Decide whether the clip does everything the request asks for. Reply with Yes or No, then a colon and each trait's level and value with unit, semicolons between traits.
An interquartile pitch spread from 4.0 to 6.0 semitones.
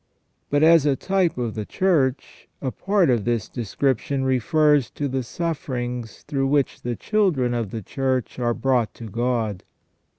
No: average, 3.6 semitones